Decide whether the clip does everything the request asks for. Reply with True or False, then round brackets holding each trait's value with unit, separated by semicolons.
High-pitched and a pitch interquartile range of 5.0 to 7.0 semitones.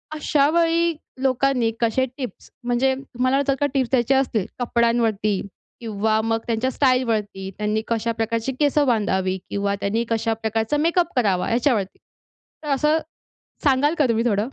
False (235 Hz; 3.7 semitones)